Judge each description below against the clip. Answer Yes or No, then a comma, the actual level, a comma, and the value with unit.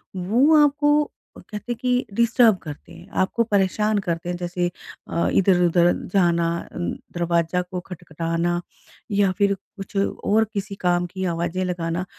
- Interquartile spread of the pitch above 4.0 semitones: No, average, 3.4 semitones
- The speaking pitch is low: No, medium, 185 Hz